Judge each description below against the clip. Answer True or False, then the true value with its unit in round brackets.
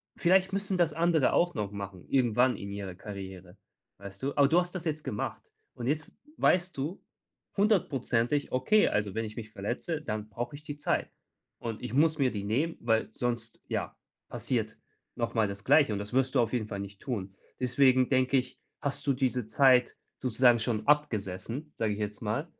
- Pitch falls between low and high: False (125 Hz)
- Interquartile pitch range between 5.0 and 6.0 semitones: True (5.6 semitones)